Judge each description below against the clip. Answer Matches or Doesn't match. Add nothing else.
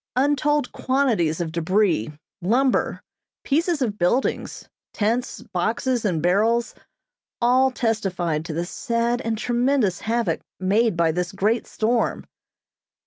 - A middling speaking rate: Doesn't match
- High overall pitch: Matches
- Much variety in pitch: Matches